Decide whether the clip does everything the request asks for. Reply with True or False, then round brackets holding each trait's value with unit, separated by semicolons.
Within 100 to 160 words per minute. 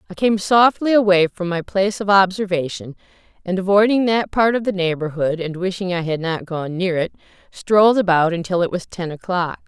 False (190 wpm)